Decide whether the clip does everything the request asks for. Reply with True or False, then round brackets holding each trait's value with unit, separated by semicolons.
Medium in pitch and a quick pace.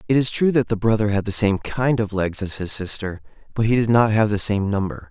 False (105 Hz; 270 wpm)